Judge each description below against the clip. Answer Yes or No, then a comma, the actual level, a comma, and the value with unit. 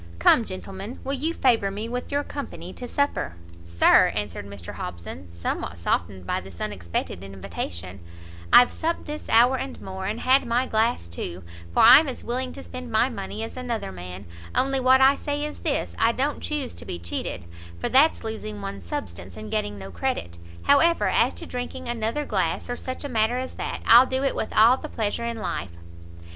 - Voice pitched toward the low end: No, high, 225 Hz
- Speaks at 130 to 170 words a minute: No, average, 195 wpm